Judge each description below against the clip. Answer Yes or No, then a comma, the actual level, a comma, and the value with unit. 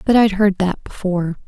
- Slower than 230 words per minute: Yes, fast, 205 wpm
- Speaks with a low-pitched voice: No, high, 195 Hz